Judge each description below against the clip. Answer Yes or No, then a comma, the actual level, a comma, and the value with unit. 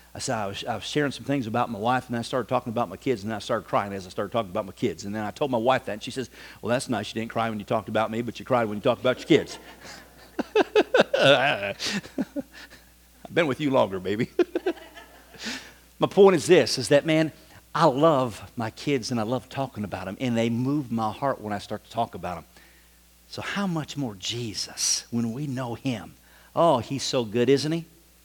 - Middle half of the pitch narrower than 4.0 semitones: No, average, 4.7 semitones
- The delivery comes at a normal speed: No, fast, 230 wpm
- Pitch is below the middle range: Yes, low, 125 Hz